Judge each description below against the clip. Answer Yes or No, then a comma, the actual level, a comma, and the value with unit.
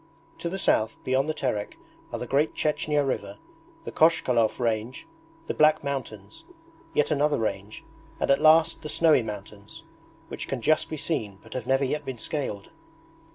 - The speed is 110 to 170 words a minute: Yes, average, 165 wpm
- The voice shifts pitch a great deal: Yes, wide, 5.7 semitones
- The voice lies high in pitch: No, low, 135 Hz